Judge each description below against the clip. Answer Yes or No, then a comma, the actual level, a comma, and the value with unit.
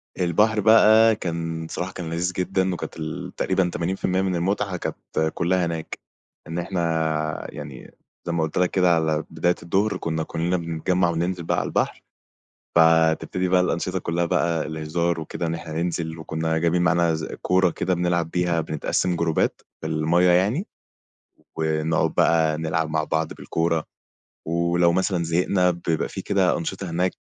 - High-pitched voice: No, very low, 85 Hz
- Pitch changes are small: Yes, narrow, 2.1 semitones